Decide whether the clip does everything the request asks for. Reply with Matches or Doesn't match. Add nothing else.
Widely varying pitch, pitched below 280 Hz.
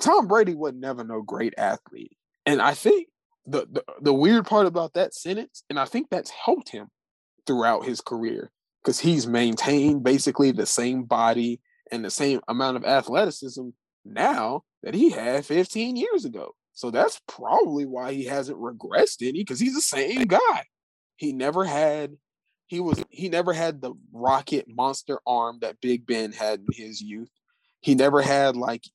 Matches